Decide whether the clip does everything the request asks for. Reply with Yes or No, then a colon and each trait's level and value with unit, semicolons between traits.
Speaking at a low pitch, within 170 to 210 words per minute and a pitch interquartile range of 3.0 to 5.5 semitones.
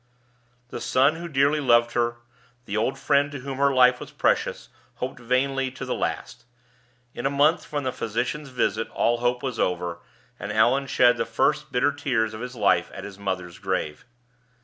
Yes: low, 125 Hz; average, 185 wpm; average, 3.9 semitones